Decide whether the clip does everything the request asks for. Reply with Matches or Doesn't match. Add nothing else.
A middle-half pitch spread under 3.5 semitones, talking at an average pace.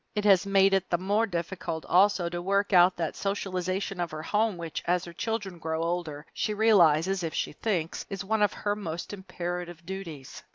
Matches